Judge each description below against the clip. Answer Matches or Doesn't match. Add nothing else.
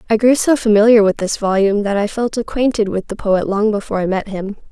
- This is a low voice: Doesn't match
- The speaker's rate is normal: Doesn't match